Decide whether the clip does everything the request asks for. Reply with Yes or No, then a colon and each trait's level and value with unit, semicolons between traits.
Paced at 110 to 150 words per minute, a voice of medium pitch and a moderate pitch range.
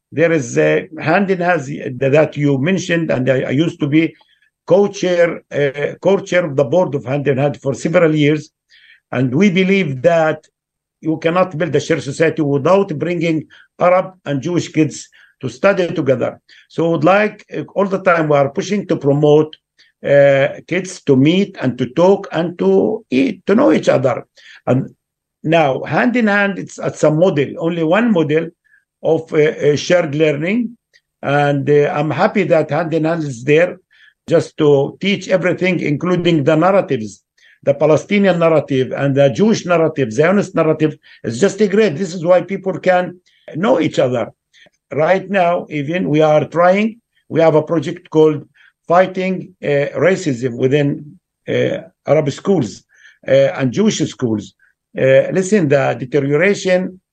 No: average, 165 wpm; medium, 160 Hz; average, 4.0 semitones